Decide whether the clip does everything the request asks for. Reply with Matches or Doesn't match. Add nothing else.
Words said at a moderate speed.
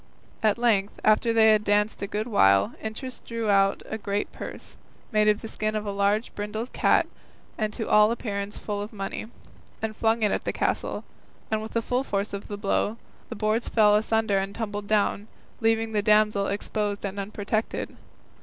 Matches